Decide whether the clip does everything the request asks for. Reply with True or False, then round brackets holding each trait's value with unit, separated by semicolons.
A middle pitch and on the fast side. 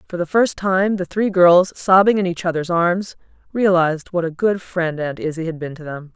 True (180 Hz; 225 wpm)